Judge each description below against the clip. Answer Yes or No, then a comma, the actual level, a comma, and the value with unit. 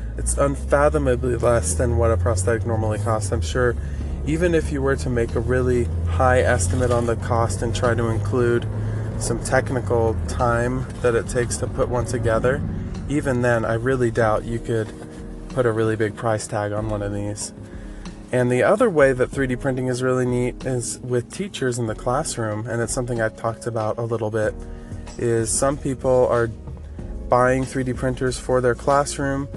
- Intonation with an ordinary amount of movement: Yes, average, 3.2 semitones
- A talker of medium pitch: No, low, 115 Hz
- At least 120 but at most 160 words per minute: No, average, 185 wpm